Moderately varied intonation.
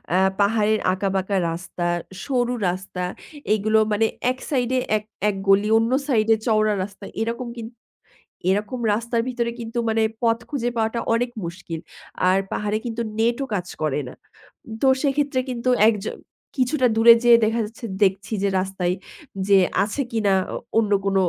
Yes: average, 3.2 semitones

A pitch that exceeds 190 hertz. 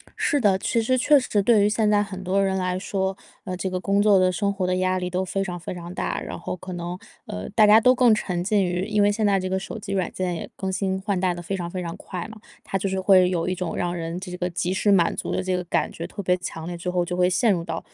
No: medium, 185 Hz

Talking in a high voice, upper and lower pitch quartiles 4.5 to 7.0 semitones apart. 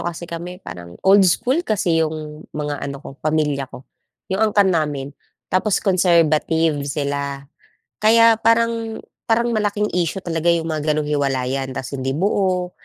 No: medium, 165 Hz; wide, 5.4 semitones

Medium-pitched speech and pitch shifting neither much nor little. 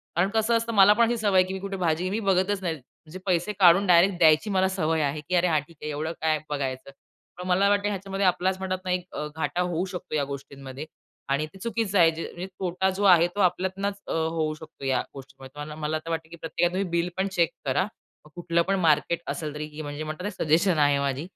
Yes: medium, 175 Hz; average, 3.6 semitones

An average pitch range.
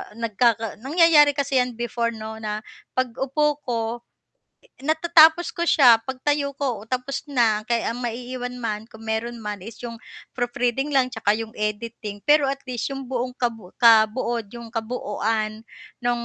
Yes: average, 3.2 semitones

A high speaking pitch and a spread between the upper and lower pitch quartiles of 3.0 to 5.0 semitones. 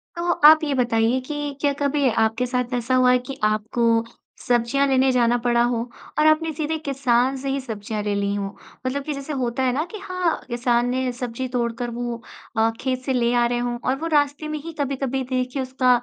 No: very high, 255 Hz; narrow, 2.6 semitones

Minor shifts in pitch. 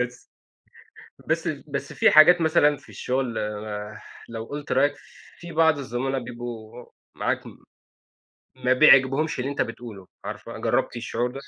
No: average, 3.2 semitones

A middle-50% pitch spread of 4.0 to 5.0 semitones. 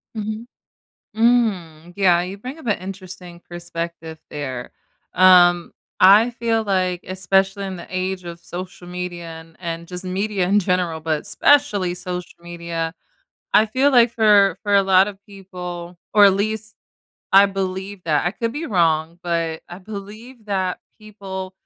No: average, 2.9 semitones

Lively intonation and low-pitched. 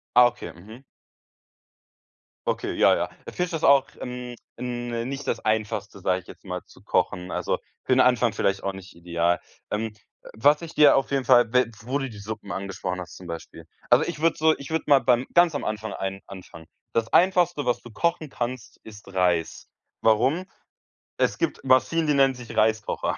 Yes: wide, 5.9 semitones; low, 120 Hz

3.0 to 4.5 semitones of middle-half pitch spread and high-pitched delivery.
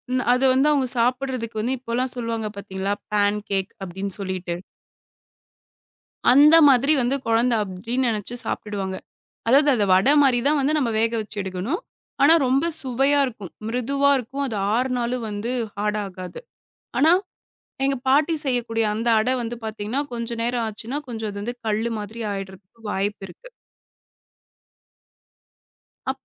Yes: average, 4.1 semitones; high, 235 Hz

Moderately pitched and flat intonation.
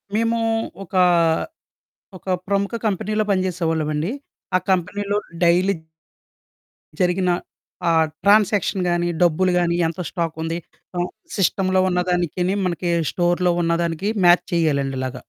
Yes: medium, 180 Hz; narrow, 2.3 semitones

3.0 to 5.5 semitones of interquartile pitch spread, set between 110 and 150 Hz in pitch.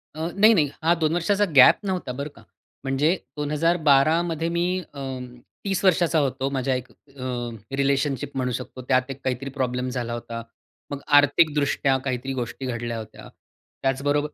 Yes: average, 3.6 semitones; medium, 140 Hz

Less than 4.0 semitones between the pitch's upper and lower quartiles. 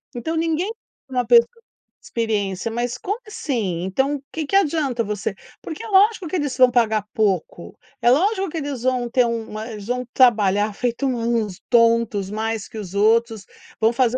No: average, 4.4 semitones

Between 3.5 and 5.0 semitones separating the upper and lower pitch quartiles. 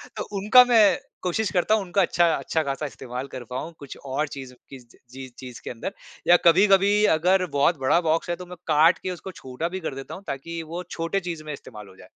No: wide, 5.4 semitones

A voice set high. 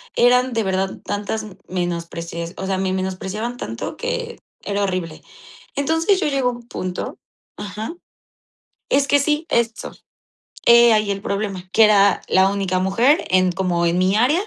Yes: high, 200 Hz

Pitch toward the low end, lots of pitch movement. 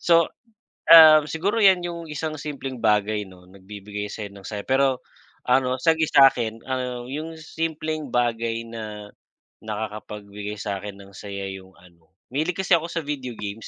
Yes: low, 120 Hz; wide, 7.0 semitones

